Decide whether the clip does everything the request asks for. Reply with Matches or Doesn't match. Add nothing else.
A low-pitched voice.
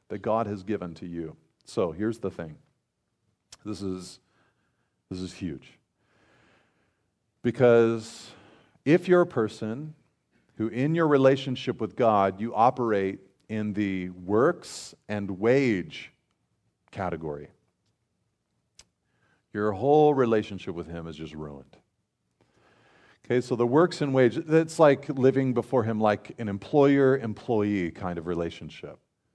Matches